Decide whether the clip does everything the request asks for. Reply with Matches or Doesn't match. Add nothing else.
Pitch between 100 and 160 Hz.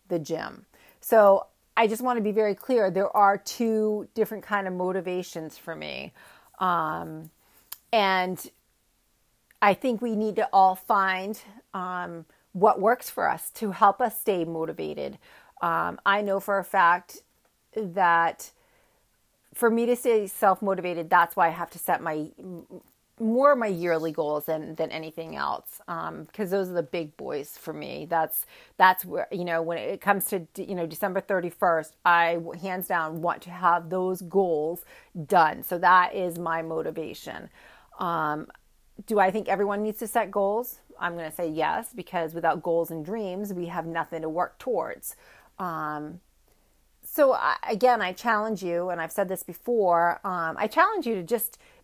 Doesn't match